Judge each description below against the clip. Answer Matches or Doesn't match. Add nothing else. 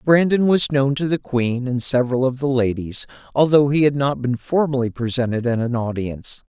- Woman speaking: Doesn't match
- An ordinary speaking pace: Matches